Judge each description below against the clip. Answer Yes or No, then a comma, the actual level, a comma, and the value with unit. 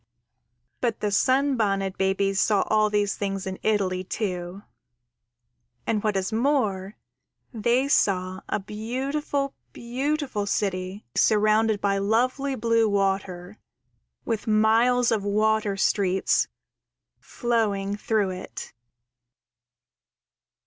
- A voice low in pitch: No, high, 210 Hz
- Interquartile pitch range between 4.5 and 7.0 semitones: No, average, 2.9 semitones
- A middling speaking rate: No, slow, 100 wpm